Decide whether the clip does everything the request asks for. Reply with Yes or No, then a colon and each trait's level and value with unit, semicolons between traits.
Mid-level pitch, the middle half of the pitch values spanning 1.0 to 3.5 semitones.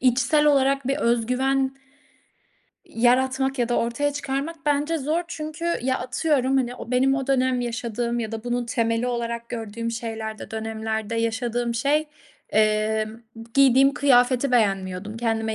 No: high, 245 Hz; average, 2.9 semitones